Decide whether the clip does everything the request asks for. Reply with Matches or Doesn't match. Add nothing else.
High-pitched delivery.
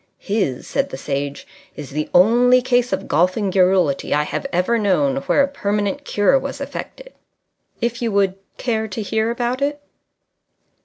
Matches